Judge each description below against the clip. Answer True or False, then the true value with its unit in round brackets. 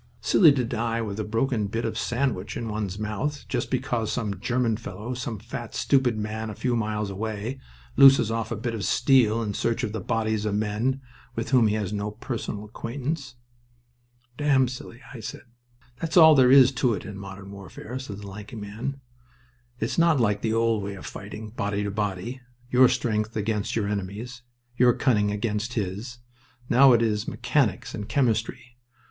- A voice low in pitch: True (110 Hz)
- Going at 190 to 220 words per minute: False (180 wpm)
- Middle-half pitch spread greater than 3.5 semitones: False (3.0 semitones)